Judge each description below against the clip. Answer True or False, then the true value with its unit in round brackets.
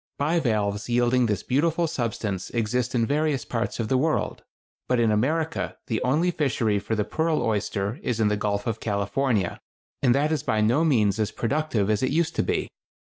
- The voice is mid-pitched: False (120 Hz)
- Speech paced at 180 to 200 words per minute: True (190 wpm)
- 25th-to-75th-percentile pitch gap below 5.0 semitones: False (5.4 semitones)